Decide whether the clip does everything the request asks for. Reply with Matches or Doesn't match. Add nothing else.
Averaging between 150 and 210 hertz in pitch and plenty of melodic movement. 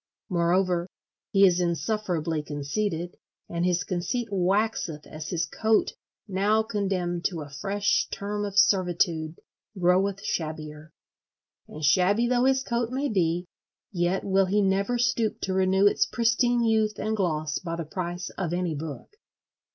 Doesn't match